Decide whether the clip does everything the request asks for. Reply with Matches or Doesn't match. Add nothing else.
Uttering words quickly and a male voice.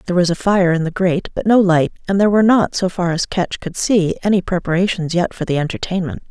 Doesn't match